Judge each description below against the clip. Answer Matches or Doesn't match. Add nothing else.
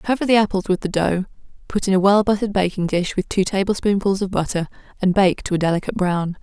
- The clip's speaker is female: Matches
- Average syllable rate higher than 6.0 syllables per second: Matches